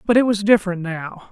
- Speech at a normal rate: No, fast, 225 wpm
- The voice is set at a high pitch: Yes, high, 195 Hz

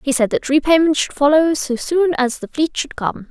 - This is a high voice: Yes, very high, 290 Hz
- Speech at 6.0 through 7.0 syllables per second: No, 5.0 syllables/s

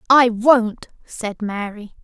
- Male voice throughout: No, female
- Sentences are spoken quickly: No, slow, 120 wpm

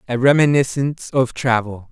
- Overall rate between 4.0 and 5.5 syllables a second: Yes, 5.2 syllables/s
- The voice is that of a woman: No, male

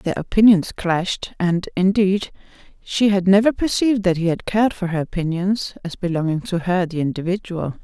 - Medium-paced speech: Yes, average, 170 wpm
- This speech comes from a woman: Yes, female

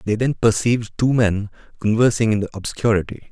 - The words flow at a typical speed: Yes, average, 165 wpm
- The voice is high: No, low, 110 Hz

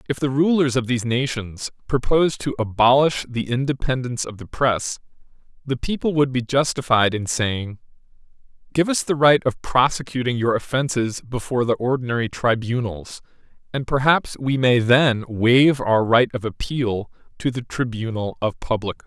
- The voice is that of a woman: No, male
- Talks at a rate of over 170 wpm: No, average, 155 wpm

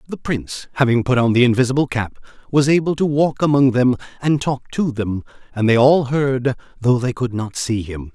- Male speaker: Yes, male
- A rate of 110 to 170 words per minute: No, fast, 205 wpm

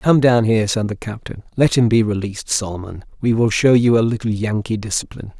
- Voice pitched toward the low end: Yes, low, 110 Hz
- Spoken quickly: Yes, fast, 210 wpm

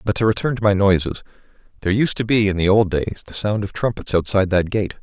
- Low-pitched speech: Yes, low, 100 Hz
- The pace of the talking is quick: Yes, fast, 250 wpm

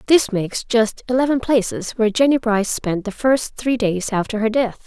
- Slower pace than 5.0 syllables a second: No, 5.2 syllables/s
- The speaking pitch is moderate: No, high, 230 Hz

